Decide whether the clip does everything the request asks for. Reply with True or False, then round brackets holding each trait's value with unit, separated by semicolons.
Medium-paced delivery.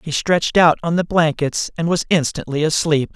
True (190 wpm)